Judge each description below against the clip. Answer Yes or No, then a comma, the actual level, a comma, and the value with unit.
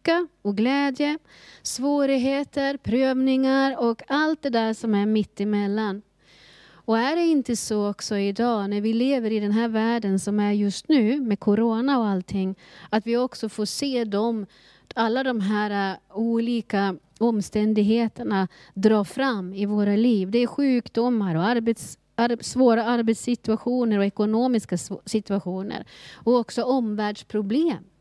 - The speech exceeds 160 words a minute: No, average, 135 wpm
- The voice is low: No, high, 225 Hz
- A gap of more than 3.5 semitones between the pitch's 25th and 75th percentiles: No, average, 3.2 semitones